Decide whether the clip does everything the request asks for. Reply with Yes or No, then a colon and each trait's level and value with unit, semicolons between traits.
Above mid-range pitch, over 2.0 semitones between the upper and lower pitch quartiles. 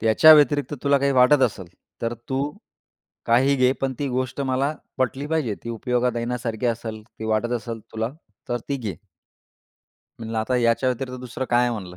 No: low, 125 Hz; average, 2.7 semitones